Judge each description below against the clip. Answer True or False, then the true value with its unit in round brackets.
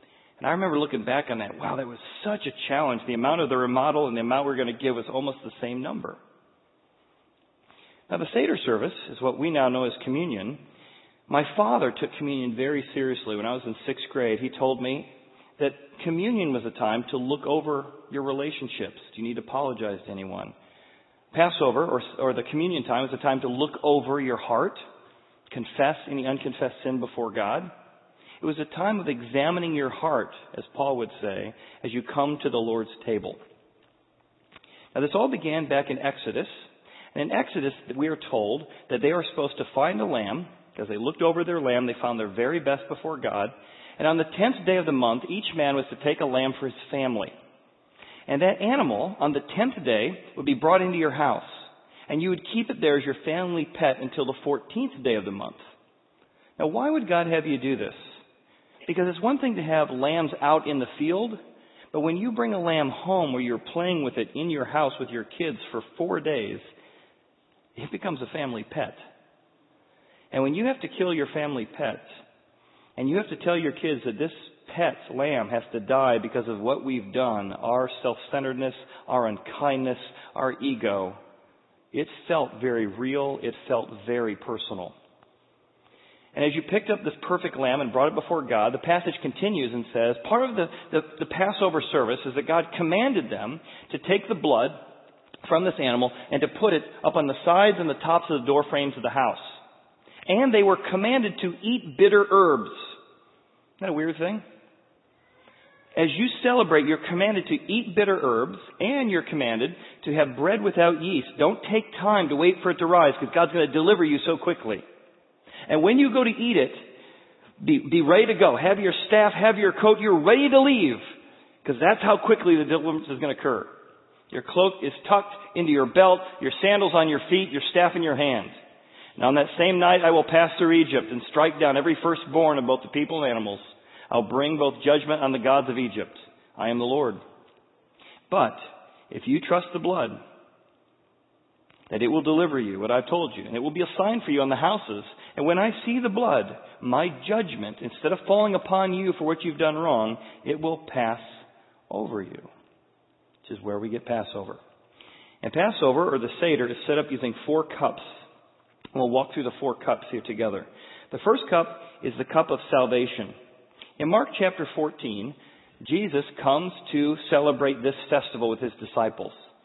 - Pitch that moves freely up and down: True (5.7 semitones)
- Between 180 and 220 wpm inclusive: True (200 wpm)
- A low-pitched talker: False (150 Hz)